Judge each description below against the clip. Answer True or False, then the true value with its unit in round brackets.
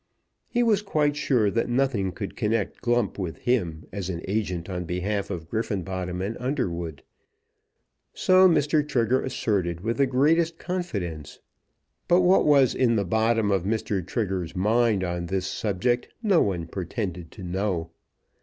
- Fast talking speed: False (150 wpm)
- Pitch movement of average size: False (6.1 semitones)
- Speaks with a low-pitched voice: True (105 Hz)